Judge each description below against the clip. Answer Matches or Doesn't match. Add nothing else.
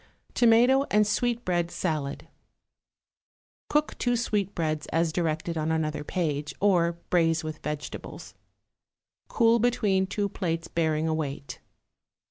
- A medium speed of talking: Doesn't match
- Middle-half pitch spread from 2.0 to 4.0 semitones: Doesn't match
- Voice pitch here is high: Doesn't match